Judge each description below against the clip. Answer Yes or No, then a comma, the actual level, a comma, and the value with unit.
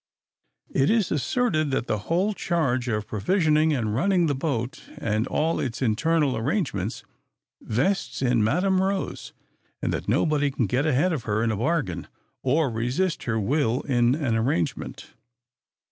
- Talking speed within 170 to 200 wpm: No, average, 150 wpm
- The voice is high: No, low, 135 Hz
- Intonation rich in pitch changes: Yes, wide, 6.2 semitones